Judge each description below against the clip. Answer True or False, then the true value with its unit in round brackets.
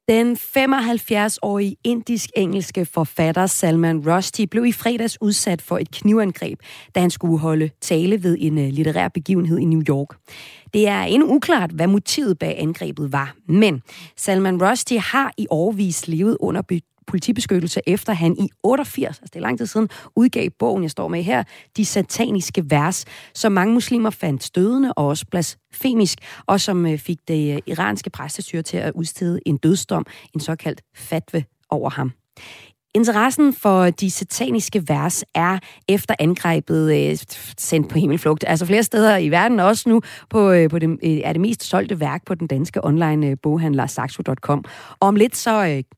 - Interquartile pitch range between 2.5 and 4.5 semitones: False (5.2 semitones)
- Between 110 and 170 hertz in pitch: False (180 Hz)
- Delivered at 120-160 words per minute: True (155 wpm)